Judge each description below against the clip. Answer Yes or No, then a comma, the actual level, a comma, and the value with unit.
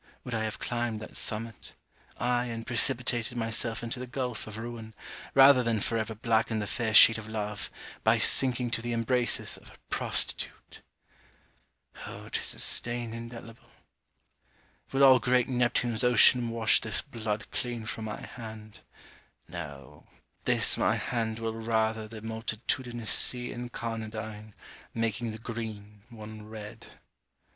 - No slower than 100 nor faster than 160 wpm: Yes, average, 140 wpm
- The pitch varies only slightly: Yes, narrow, 1.7 semitones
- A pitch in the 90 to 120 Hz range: Yes, low, 115 Hz